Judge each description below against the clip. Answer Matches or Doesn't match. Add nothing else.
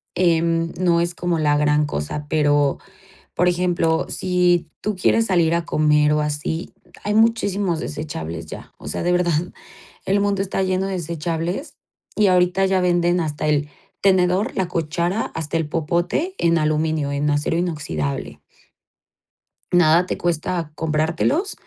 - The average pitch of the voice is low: Doesn't match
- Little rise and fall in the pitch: Doesn't match